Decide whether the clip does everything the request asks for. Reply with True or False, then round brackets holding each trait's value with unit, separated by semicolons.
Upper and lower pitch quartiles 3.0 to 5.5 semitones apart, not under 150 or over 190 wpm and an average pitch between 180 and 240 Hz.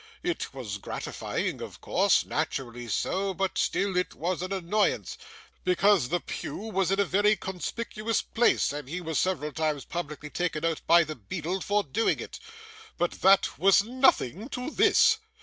True (4.8 semitones; 165 wpm; 185 Hz)